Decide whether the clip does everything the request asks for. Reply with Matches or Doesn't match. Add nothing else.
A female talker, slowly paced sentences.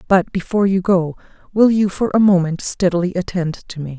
Doesn't match